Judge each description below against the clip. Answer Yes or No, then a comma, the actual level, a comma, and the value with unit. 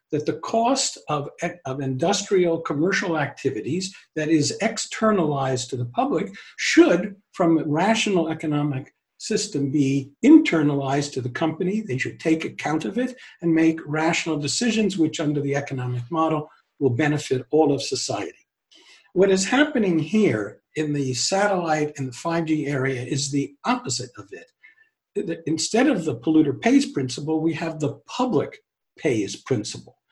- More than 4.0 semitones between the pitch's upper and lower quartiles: Yes, average, 5.3 semitones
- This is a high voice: No, medium, 160 Hz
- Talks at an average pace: Yes, average, 145 wpm